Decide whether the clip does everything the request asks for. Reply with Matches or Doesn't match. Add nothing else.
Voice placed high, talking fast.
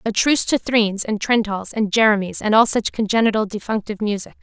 Doesn't match